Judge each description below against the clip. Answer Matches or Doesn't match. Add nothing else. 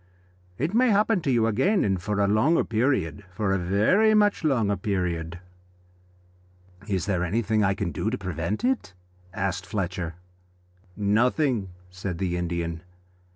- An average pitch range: Doesn't match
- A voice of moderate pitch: Doesn't match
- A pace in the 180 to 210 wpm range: Doesn't match